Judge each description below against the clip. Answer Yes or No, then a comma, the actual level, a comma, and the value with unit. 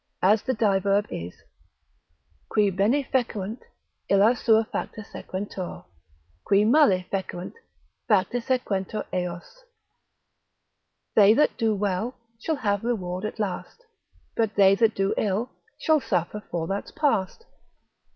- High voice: Yes, high, 205 Hz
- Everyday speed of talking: No, slow, 115 wpm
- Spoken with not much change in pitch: No, average, 3.1 semitones